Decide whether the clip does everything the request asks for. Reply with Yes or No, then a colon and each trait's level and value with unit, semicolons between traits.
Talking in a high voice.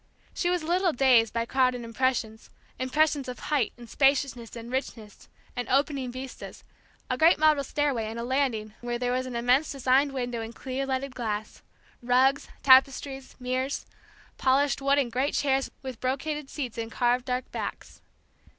Yes: very high, 260 Hz